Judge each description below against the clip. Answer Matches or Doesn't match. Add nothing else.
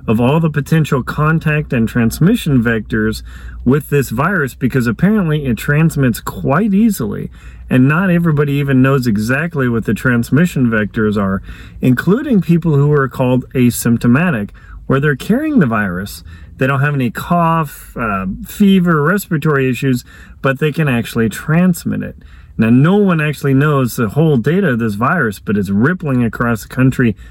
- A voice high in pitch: Doesn't match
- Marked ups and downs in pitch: Matches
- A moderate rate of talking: Matches